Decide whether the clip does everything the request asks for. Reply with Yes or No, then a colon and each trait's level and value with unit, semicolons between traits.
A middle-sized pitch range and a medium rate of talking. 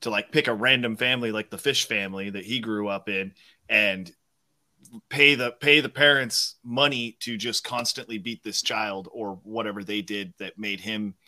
Yes: average, 3.7 semitones; average, 185 wpm